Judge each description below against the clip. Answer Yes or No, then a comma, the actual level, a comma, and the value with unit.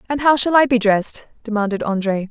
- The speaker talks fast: Yes, fast, 210 wpm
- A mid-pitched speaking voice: No, high, 230 Hz